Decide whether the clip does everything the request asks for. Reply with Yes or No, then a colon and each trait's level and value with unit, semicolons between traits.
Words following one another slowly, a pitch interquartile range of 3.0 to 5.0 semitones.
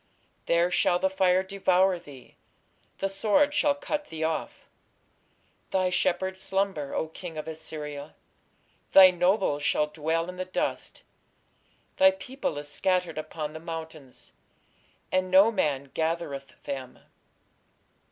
Yes: slow, 125 wpm; average, 3.6 semitones